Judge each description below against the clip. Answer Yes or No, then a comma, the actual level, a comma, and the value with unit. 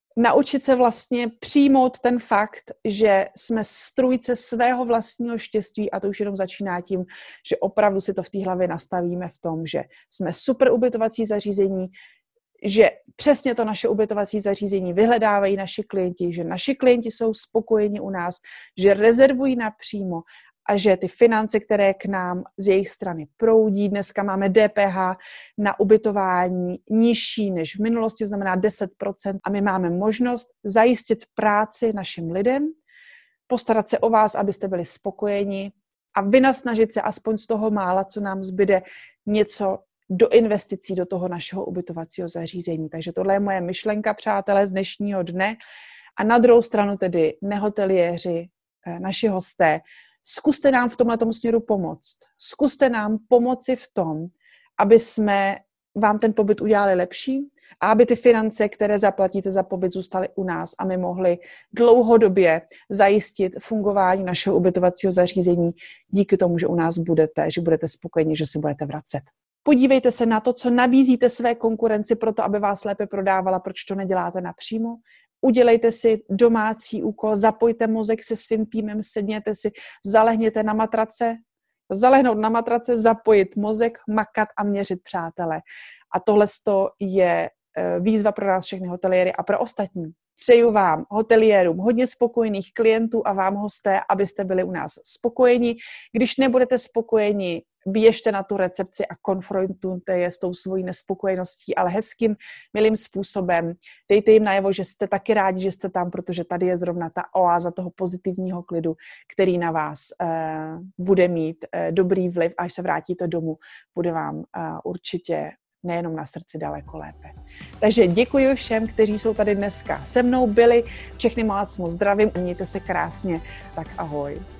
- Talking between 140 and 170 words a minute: Yes, average, 155 wpm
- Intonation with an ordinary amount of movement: Yes, average, 3.5 semitones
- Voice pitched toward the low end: No, high, 205 Hz